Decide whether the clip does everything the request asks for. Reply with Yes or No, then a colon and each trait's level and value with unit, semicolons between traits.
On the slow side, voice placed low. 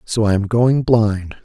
No: fast, 210 wpm; low, 110 Hz